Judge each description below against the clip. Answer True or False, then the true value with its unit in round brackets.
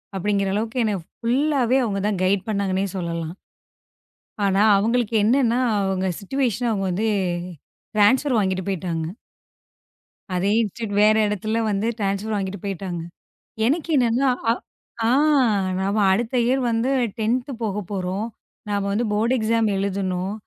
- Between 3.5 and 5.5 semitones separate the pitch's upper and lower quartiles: False (3.1 semitones)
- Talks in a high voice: True (205 Hz)